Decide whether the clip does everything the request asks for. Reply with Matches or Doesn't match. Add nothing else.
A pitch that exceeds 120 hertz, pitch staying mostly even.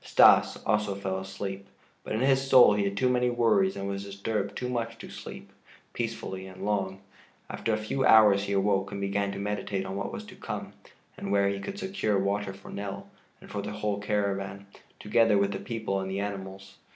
Doesn't match